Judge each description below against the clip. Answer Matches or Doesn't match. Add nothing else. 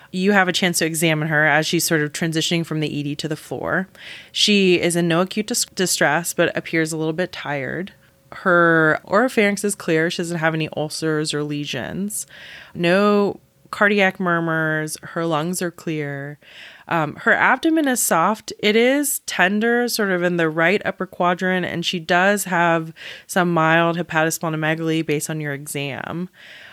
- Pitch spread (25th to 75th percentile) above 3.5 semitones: Doesn't match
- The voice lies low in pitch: Doesn't match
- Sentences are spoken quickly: Doesn't match